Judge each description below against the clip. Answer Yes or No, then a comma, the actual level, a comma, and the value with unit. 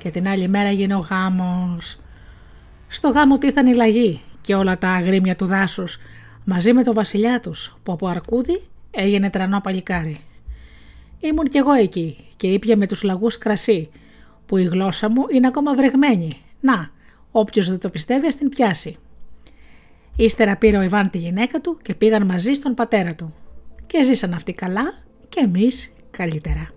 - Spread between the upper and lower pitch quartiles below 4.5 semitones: No, average, 5.2 semitones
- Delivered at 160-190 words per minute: Yes, average, 165 wpm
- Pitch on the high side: Yes, high, 195 Hz